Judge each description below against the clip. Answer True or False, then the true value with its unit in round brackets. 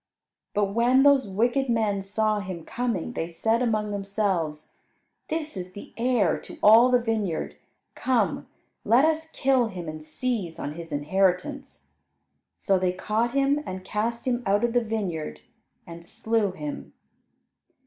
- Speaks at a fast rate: False (150 wpm)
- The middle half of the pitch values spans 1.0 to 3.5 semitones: False (4.7 semitones)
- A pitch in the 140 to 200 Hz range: False (215 Hz)